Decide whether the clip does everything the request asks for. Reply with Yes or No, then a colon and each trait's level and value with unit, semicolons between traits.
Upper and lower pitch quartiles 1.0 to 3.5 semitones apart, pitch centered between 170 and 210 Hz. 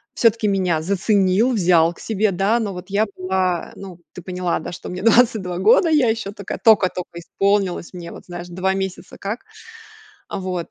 Yes: average, 2.8 semitones; high, 190 Hz